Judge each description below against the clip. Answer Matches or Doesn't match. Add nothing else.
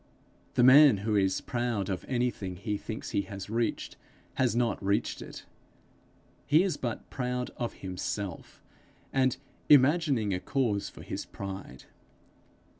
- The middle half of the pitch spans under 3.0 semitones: Doesn't match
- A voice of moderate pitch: Doesn't match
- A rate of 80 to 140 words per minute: Matches